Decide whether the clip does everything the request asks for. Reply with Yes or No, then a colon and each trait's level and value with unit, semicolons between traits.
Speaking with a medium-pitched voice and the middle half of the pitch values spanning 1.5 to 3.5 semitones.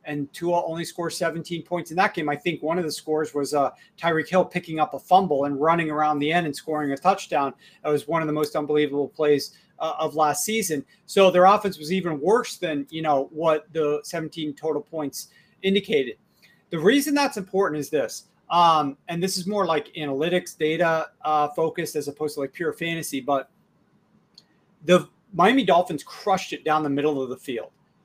Yes: medium, 160 Hz; average, 3.2 semitones